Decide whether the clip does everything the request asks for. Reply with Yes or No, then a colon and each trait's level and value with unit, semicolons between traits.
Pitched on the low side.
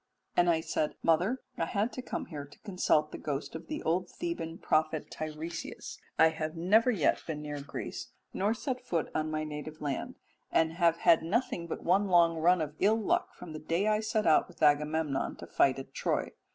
No: medium, 165 Hz